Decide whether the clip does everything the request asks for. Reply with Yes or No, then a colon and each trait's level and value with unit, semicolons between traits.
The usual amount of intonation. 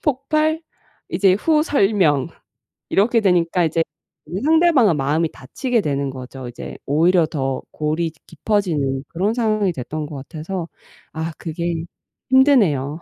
No: wide, 6.8 semitones